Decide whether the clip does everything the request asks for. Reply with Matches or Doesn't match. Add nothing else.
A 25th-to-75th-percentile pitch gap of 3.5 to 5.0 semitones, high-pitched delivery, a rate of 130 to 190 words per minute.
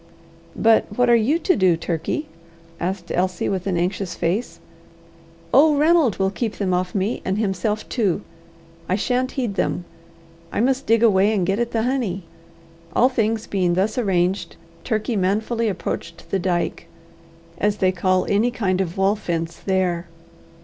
Matches